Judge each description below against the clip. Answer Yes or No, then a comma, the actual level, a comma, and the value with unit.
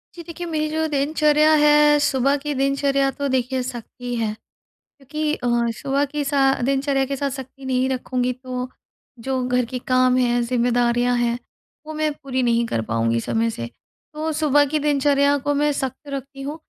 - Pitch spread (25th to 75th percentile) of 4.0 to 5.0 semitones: No, average, 2.7 semitones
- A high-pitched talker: Yes, very high, 270 Hz